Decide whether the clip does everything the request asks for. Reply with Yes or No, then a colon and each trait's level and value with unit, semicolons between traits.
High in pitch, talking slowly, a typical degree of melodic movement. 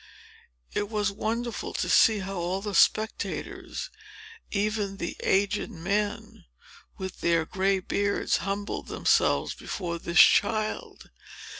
No: high, 200 Hz; slow, 115 wpm; narrow, 2.0 semitones